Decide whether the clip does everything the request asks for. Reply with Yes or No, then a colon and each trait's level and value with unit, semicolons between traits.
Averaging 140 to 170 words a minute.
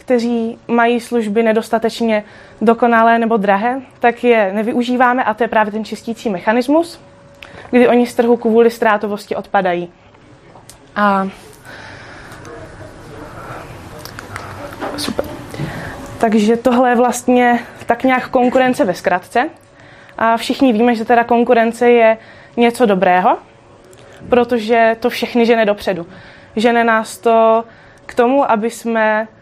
No: slow, 115 wpm